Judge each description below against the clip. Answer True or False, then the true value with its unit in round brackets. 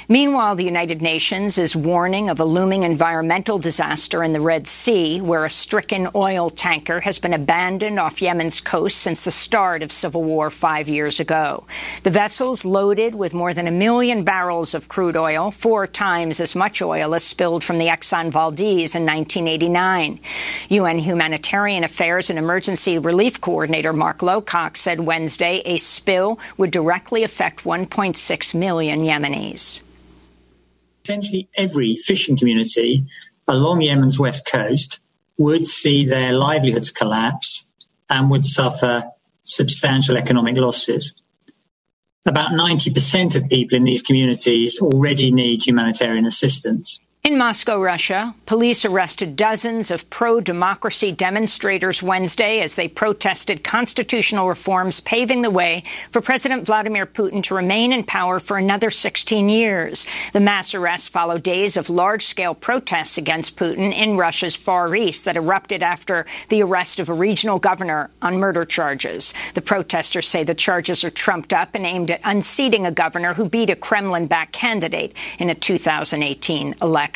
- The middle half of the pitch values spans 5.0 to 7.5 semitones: False (3.8 semitones)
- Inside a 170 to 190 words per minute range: False (145 wpm)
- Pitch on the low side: False (175 Hz)